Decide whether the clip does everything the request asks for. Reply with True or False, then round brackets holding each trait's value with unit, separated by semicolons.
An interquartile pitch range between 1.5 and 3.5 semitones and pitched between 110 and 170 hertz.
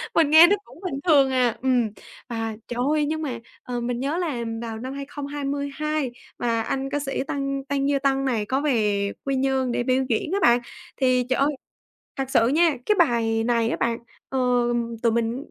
False (3.0 semitones; 265 Hz)